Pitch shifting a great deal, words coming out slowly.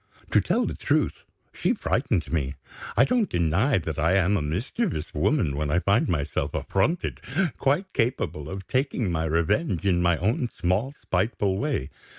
No: wide, 7.4 semitones; average, 165 wpm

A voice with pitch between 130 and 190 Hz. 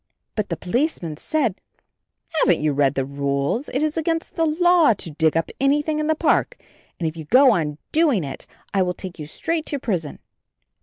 No: high, 205 Hz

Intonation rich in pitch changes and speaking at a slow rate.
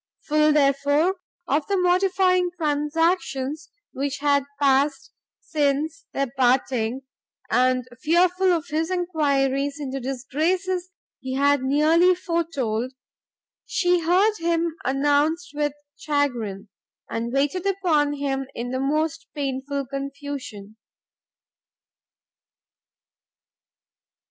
No: average, 3.8 semitones; slow, 95 wpm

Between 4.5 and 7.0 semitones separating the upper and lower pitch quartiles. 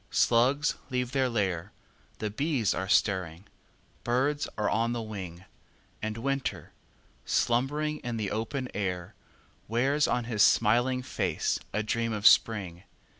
No: average, 3.8 semitones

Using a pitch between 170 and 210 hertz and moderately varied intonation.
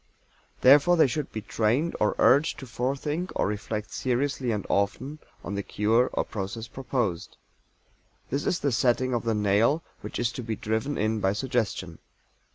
No: low, 120 Hz; average, 4.4 semitones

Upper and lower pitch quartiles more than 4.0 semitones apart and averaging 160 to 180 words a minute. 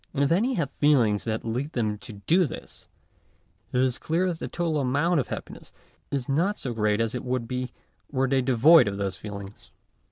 No: average, 5.2 semitones; average, 200 wpm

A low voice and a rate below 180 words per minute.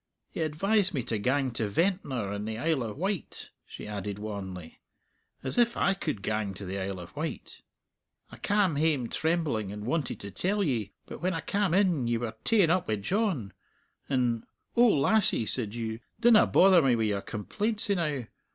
No: low, 130 Hz; average, 185 wpm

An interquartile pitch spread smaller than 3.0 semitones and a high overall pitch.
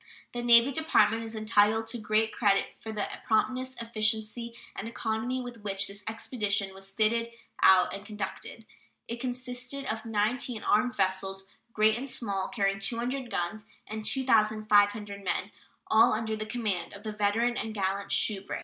Yes: narrow, 2.4 semitones; high, 220 Hz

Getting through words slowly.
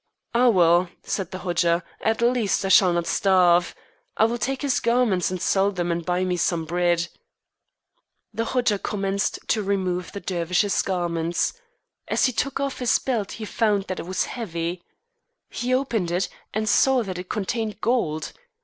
No: average, 170 wpm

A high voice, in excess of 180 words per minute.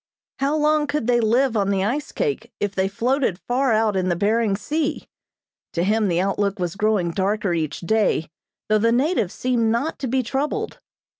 Yes: high, 220 Hz; average, 190 wpm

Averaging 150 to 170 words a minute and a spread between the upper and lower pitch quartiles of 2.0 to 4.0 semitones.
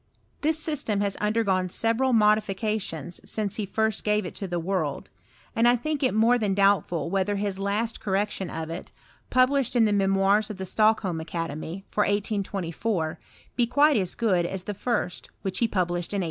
No: average, 190 wpm; average, 3.2 semitones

